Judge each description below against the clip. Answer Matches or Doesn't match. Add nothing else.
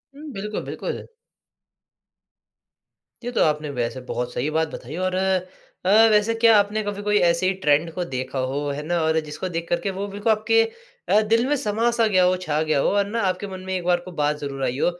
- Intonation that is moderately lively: Doesn't match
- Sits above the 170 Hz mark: Matches